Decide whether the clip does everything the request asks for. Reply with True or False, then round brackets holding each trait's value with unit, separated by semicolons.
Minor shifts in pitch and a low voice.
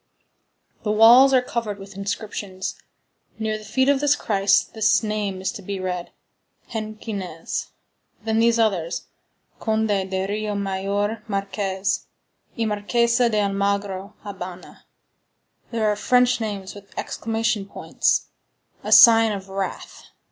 False (2.3 semitones; 205 Hz)